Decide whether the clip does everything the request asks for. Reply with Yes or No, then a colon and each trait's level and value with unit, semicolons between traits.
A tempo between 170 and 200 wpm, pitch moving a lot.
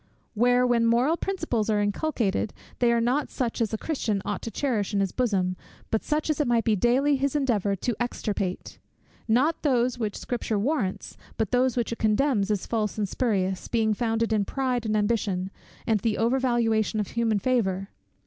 No: average, 185 wpm; average, 3.1 semitones